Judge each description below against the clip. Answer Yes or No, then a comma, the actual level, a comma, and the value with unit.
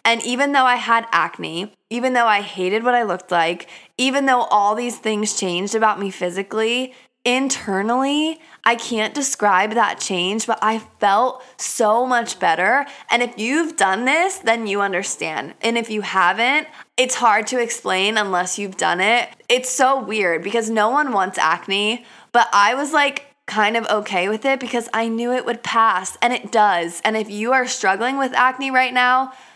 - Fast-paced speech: No, average, 185 wpm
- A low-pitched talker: No, high, 230 Hz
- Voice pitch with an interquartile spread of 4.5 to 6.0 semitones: No, average, 3.6 semitones